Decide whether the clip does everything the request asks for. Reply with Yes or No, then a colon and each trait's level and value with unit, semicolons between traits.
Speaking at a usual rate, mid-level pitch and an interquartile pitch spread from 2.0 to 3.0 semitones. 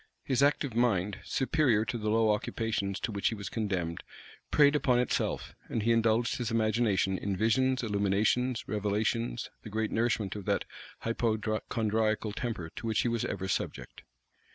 No: average, 155 wpm; low, 110 Hz; narrow, 2.4 semitones